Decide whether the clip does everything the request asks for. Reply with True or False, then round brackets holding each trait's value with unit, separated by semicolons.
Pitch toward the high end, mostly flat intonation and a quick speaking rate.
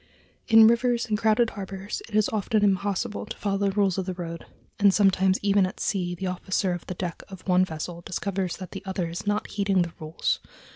True (195 Hz; 2.2 semitones; 210 wpm)